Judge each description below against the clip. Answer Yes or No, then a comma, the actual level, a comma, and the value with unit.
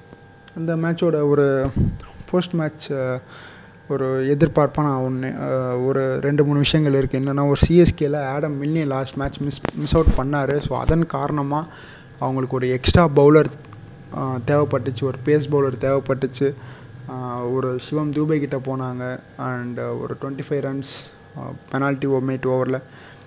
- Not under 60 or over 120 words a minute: No, fast, 130 wpm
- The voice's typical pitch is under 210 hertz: Yes, low, 135 Hz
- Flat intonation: Yes, narrow, 2.2 semitones